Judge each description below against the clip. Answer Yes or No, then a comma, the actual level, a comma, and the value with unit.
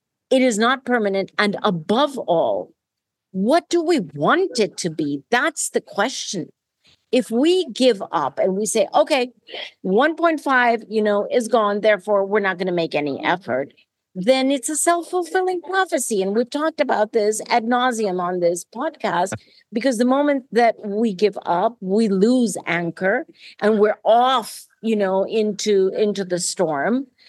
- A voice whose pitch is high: Yes, high, 220 Hz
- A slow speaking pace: No, average, 160 wpm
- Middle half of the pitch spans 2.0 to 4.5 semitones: No, average, 5.0 semitones